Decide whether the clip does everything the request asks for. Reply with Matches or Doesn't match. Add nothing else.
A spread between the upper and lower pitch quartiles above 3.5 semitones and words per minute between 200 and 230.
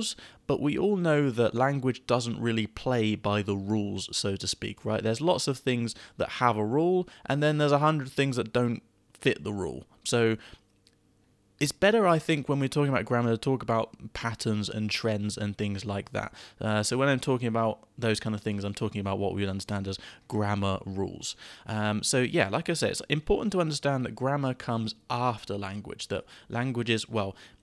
Matches